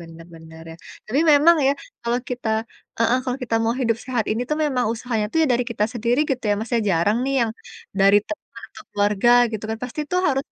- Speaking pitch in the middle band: No, high, 235 Hz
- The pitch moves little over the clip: No, average, 3.4 semitones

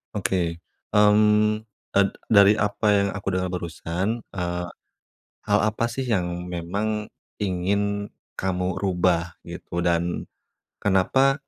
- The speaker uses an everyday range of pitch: Yes, average, 3.0 semitones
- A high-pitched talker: No, low, 100 Hz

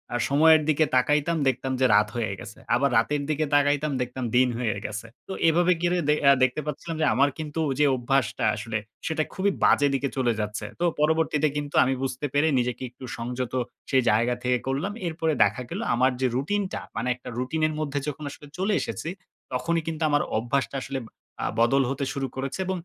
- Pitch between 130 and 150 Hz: Yes, medium, 140 Hz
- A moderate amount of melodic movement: Yes, average, 3.8 semitones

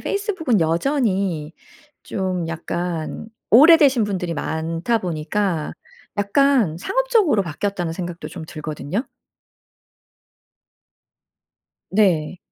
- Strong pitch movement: Yes, wide, 6.4 semitones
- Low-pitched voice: No, high, 190 Hz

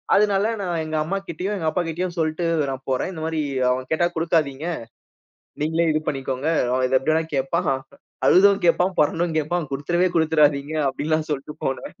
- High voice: No, medium, 160 Hz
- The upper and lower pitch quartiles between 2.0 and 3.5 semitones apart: Yes, average, 3.2 semitones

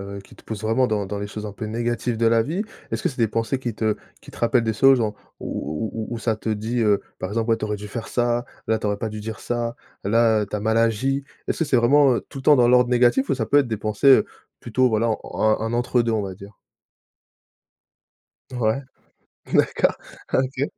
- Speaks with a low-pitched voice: Yes, low, 115 Hz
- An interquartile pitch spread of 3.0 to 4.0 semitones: No, narrow, 2.4 semitones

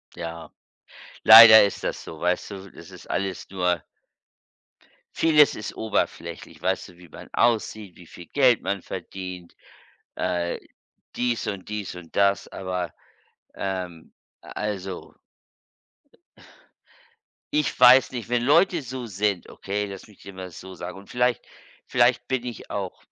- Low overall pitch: Yes, low, 100 Hz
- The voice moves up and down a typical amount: Yes, average, 4.6 semitones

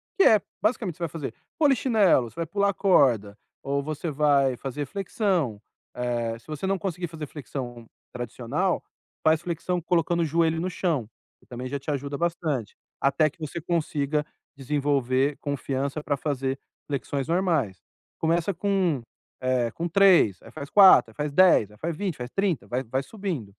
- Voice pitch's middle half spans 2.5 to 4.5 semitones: No, average, 4.9 semitones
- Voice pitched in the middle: Yes, medium, 150 Hz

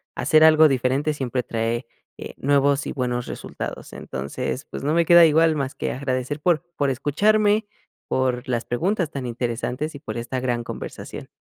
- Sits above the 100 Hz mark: Yes, low, 135 Hz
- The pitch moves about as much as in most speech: Yes, average, 4.0 semitones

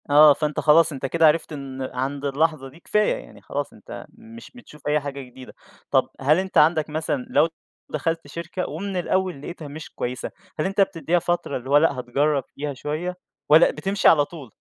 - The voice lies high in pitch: No, medium, 155 Hz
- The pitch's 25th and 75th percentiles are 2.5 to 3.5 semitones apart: Yes, average, 3.2 semitones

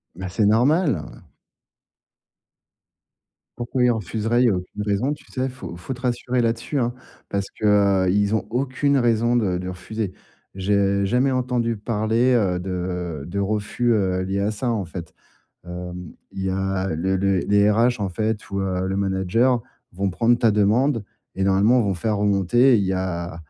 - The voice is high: No, low, 105 Hz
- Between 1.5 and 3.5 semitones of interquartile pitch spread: No, average, 4.0 semitones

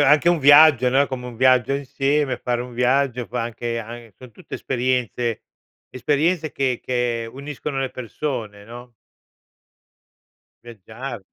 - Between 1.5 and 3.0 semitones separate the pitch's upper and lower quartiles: Yes, average, 2.7 semitones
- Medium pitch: No, low, 125 Hz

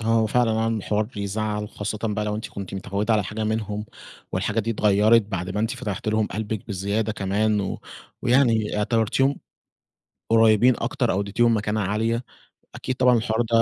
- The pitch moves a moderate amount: No, narrow, 1.6 semitones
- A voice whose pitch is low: Yes, low, 110 Hz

